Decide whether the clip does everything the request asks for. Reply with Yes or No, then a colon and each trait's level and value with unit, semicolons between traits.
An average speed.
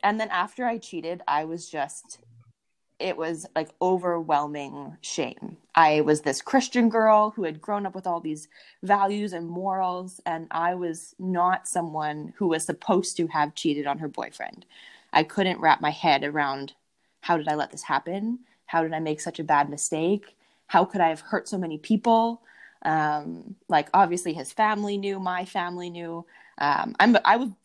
Yes: average, 175 wpm